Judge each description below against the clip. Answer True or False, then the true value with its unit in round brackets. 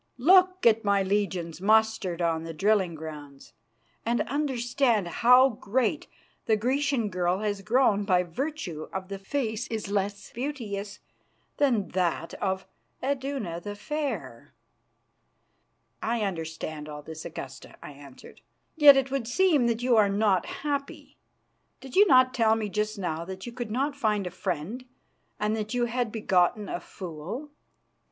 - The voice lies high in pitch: True (215 Hz)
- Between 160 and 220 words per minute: False (150 wpm)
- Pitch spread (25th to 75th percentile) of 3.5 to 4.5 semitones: False (5.3 semitones)